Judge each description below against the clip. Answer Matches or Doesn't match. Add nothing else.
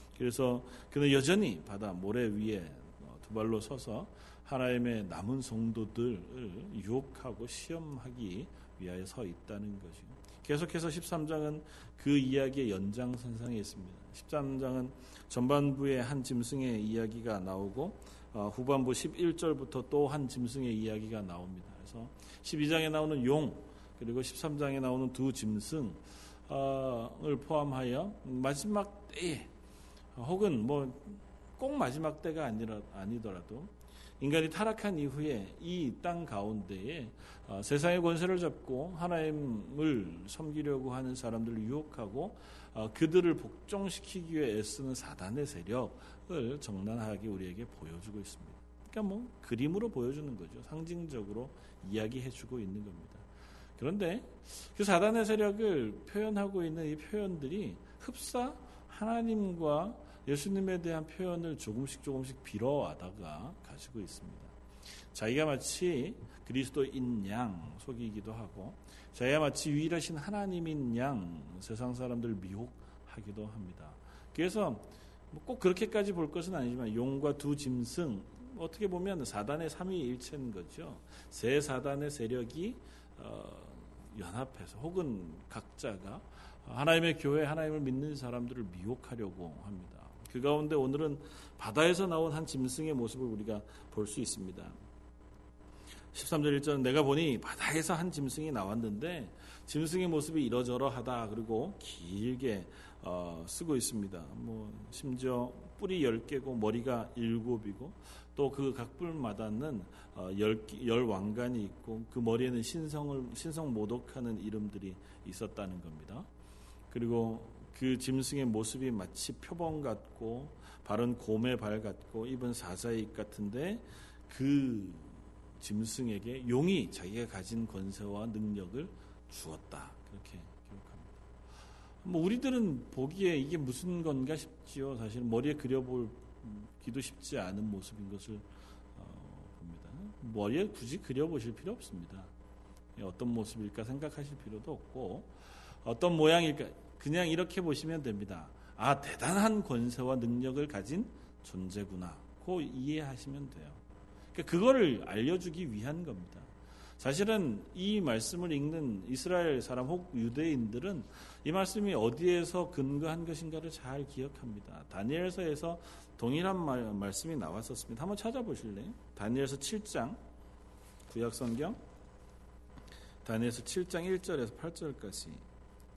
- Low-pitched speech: Matches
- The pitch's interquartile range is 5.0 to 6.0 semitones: Doesn't match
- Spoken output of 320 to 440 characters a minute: Doesn't match